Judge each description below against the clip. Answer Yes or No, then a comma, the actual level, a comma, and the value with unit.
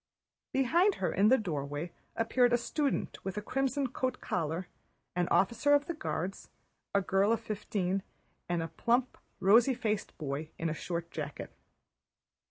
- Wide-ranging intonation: Yes, wide, 6.5 semitones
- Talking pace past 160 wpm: No, average, 155 wpm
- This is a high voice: Yes, high, 210 Hz